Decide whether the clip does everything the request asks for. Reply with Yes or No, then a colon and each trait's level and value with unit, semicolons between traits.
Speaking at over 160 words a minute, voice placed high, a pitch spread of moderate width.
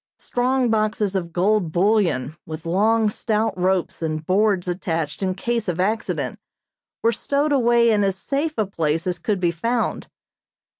No: average, 155 wpm; high, 200 Hz; average, 4.4 semitones